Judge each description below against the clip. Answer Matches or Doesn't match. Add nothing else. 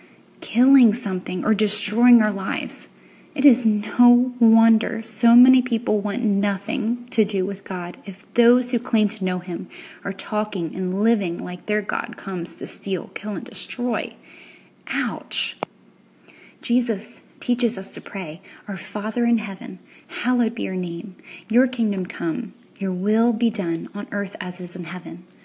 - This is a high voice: Matches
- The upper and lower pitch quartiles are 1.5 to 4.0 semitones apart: Matches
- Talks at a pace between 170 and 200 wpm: Doesn't match